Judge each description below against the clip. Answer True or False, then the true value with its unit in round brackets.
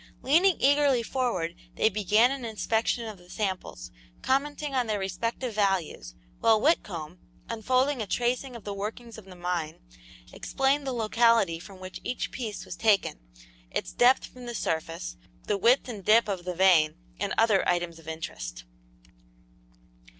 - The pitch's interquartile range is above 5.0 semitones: True (5.4 semitones)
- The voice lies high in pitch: True (215 Hz)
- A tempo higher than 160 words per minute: False (155 wpm)